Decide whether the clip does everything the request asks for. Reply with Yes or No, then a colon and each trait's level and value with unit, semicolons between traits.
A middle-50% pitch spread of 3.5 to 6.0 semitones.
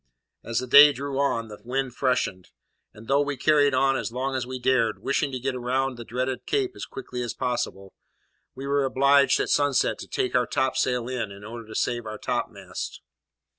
No: narrow, 2.5 semitones